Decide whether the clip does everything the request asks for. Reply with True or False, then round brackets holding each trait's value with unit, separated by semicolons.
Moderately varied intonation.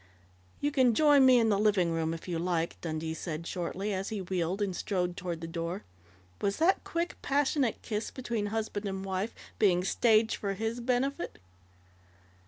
True (5.0 semitones)